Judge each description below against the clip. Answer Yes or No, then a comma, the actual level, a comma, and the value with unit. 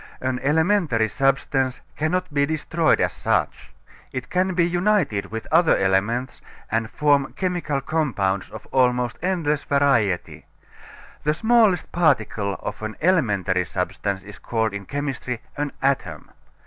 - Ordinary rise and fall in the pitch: No, wide, 6.5 semitones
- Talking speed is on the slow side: Yes, slow, 130 wpm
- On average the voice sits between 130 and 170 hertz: Yes, low, 135 Hz